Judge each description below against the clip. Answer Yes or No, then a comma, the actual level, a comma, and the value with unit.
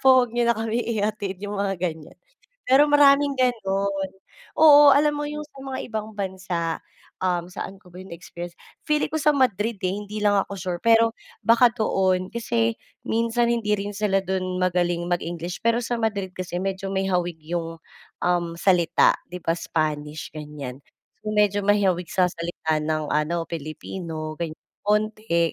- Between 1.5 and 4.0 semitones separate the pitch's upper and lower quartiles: No, average, 4.8 semitones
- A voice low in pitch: No, high, 195 Hz